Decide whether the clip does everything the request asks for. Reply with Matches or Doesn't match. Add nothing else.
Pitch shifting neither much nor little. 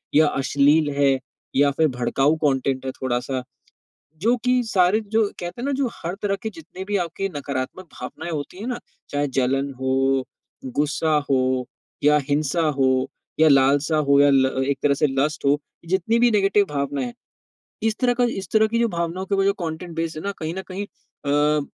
Doesn't match